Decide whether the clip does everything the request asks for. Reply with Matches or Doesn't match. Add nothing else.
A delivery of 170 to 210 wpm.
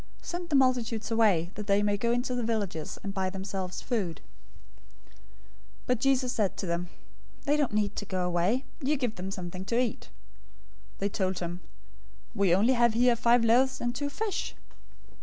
Matches